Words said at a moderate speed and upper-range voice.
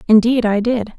Yes: average, 180 wpm; high, 225 Hz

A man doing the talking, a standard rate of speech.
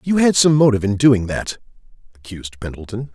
Yes: male; average, 170 wpm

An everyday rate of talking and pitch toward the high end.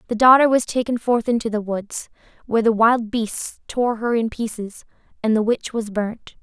Yes: average, 195 wpm; high, 225 Hz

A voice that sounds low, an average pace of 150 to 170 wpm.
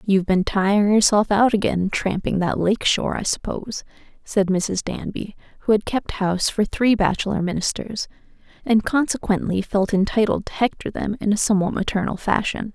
No: high, 205 Hz; average, 165 wpm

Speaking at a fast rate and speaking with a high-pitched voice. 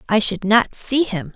Yes: fast, 220 wpm; high, 225 Hz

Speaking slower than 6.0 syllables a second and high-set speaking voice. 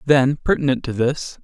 No: 4.8 syllables/s; low, 135 Hz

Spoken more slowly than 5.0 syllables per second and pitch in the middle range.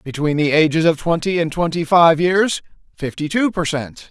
Yes: 4.8 syllables/s; medium, 165 Hz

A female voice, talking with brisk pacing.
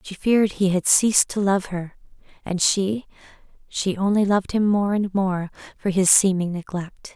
No: female; average, 170 wpm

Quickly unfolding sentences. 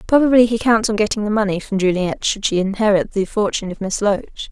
Yes: fast, 225 wpm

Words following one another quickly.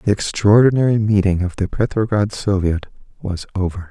No: average, 140 wpm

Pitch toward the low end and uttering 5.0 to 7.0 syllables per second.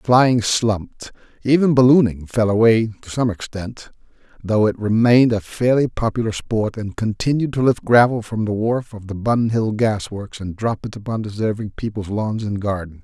No: low, 110 Hz; 4.8 syllables/s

